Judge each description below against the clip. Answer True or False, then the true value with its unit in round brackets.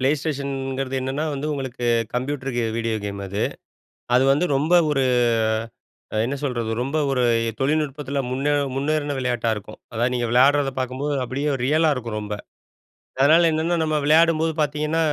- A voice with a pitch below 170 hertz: True (135 Hz)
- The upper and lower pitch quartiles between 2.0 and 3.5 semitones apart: True (2.9 semitones)